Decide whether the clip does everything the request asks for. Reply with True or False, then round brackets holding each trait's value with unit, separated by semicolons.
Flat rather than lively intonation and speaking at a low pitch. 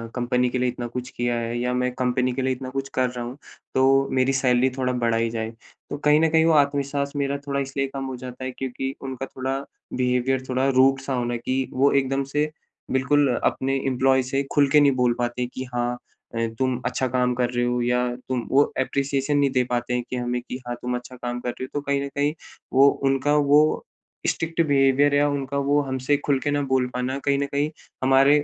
True (1.9 semitones; 130 Hz)